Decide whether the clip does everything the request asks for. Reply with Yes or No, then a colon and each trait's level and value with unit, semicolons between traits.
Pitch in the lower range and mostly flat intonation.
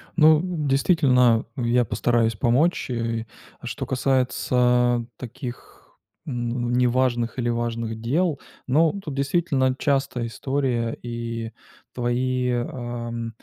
Yes: low, 125 Hz; narrow, 2.1 semitones